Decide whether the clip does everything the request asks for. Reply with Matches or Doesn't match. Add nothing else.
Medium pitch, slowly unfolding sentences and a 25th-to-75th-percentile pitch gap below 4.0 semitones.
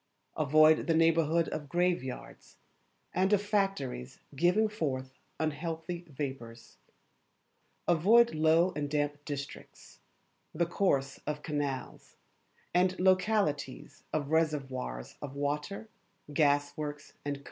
Matches